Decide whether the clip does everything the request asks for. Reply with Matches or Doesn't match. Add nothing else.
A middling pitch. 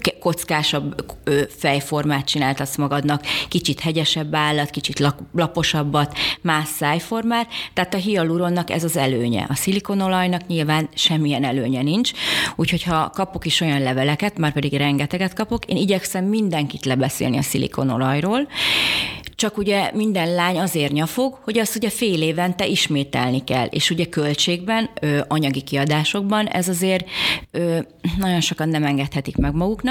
Matches